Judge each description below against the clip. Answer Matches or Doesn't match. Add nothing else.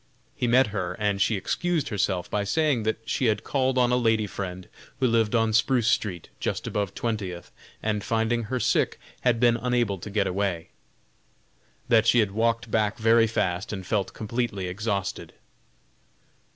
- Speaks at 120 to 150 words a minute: Doesn't match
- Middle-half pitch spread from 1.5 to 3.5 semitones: Matches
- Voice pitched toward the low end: Matches